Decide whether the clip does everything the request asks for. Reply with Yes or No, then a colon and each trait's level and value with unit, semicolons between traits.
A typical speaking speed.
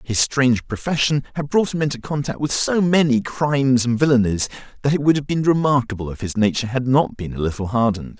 No: fast, 210 wpm